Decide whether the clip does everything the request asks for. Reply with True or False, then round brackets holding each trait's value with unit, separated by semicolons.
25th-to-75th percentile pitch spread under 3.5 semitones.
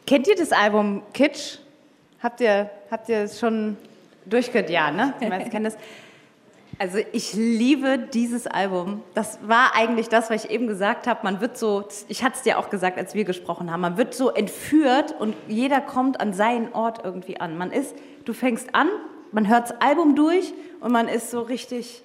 False (3.8 semitones)